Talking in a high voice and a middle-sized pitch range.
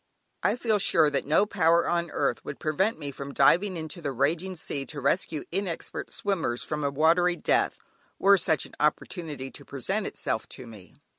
No: medium, 160 Hz; average, 4.5 semitones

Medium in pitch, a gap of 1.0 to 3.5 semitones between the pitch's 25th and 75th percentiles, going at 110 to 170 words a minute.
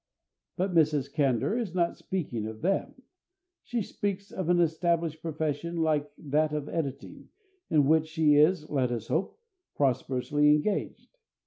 Yes: medium, 155 Hz; average, 3.1 semitones; average, 140 wpm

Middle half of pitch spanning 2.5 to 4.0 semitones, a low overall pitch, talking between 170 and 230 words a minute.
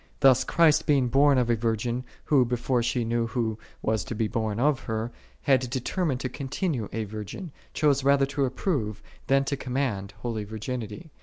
Yes: average, 3.6 semitones; low, 125 Hz; average, 180 wpm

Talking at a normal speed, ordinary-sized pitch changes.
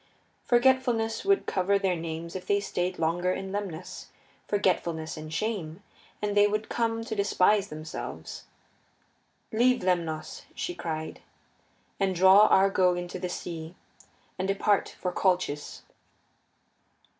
No: slow, 120 wpm; average, 3.5 semitones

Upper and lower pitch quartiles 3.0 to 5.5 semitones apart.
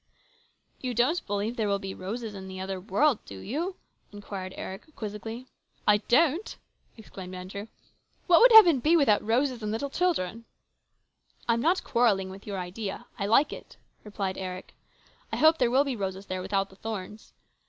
Yes: average, 5.1 semitones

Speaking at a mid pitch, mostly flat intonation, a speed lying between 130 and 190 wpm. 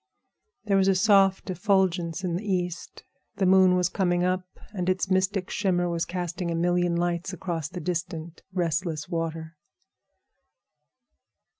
Yes: medium, 180 Hz; narrow, 1.7 semitones; average, 140 wpm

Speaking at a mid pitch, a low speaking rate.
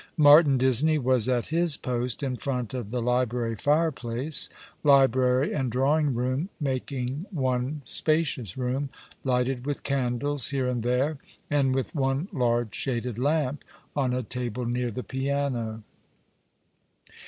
No: low, 130 Hz; slow, 130 wpm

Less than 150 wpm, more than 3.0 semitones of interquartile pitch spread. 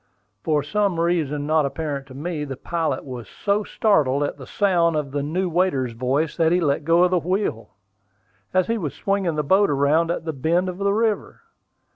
No: average, 195 wpm; average, 4.3 semitones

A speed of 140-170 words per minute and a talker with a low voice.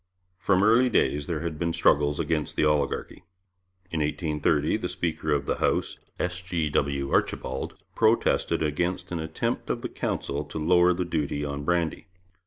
Yes: average, 165 wpm; very low, 80 Hz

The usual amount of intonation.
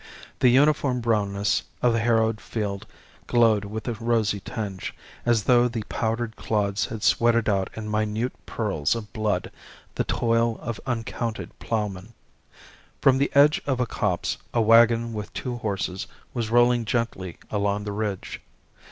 No: narrow, 2.3 semitones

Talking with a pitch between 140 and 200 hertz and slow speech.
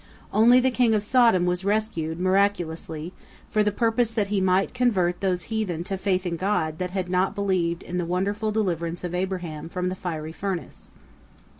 No: medium, 185 Hz; average, 180 wpm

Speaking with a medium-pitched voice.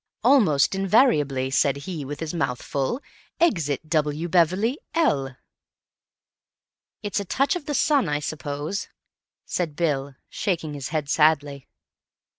Yes: medium, 155 Hz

